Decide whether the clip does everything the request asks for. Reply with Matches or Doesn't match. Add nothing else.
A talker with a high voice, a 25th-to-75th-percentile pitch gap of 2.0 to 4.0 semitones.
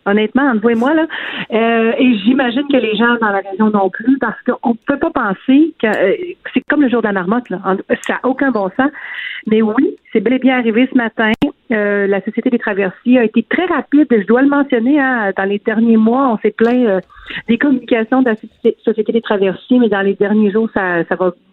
Matches